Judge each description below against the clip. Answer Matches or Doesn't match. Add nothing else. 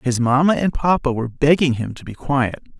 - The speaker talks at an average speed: Doesn't match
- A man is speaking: Matches